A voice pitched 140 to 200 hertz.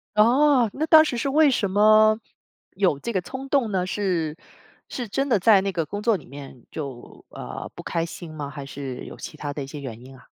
Yes: high, 190 Hz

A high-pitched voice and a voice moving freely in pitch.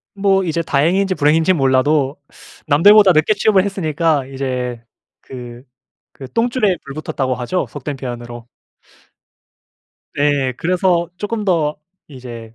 No: medium, 150 Hz; wide, 6.1 semitones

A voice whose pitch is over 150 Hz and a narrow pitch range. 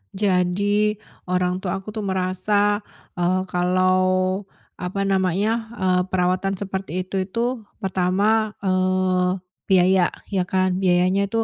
Yes: medium, 185 Hz; narrow, 1.6 semitones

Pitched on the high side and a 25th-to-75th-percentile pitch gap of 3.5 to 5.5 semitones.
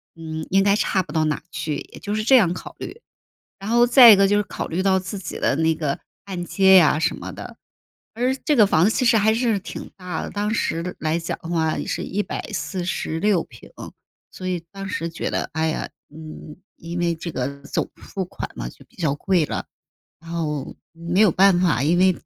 No: medium, 180 Hz; average, 3.9 semitones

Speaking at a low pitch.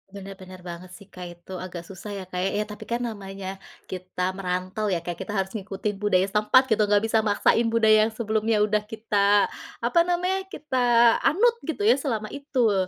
No: high, 210 Hz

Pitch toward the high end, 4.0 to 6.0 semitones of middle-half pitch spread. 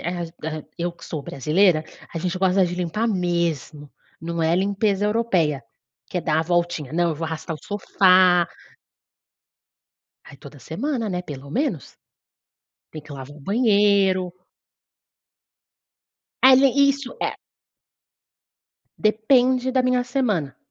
No: medium, 180 Hz; average, 5.1 semitones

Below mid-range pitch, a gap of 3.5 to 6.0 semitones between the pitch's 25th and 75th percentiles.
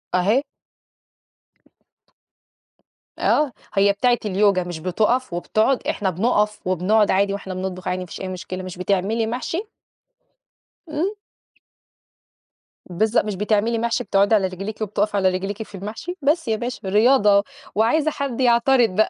No: high, 210 Hz; average, 3.9 semitones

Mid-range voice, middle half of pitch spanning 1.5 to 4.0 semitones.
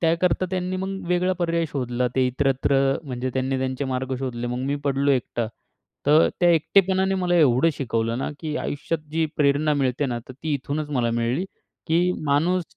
No: medium, 145 Hz; average, 4.6 semitones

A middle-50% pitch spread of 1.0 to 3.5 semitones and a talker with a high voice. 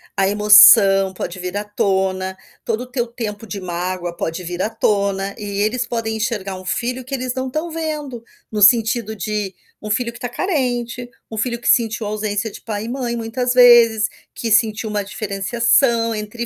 Yes: average, 3.2 semitones; high, 220 Hz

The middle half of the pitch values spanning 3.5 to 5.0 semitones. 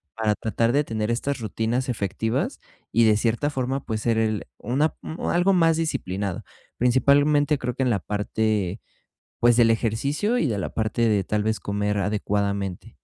Yes: average, 4.1 semitones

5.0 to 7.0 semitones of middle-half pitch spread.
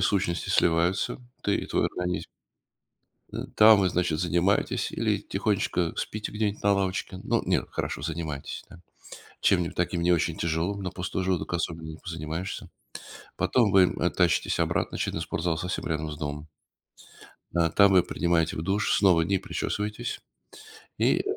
No: average, 2.8 semitones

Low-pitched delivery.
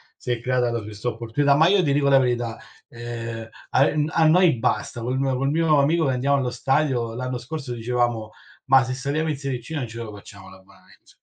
Yes: low, 130 Hz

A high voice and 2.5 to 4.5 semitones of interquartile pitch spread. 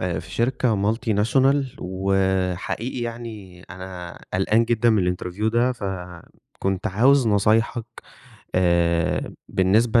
No: low, 100 Hz; average, 4.2 semitones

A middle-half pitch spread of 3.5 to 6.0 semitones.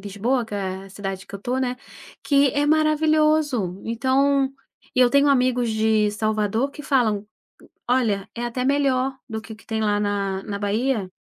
Yes: average, 4.7 semitones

